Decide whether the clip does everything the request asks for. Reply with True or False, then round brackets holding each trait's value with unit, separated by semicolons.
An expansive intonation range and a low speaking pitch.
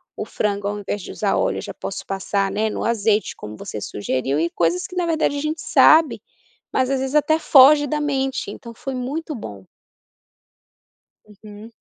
False (6.7 semitones; 235 Hz)